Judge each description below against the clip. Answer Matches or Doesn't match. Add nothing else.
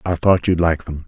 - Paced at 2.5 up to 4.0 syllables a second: Doesn't match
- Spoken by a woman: Doesn't match